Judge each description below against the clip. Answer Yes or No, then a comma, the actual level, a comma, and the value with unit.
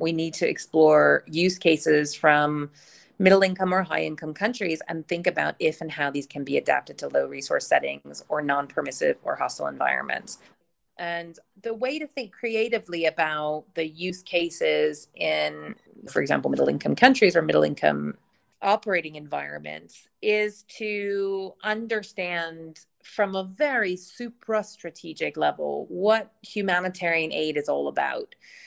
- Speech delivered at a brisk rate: No, average, 145 wpm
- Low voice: No, medium, 170 Hz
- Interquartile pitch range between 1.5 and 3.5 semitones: No, wide, 5.4 semitones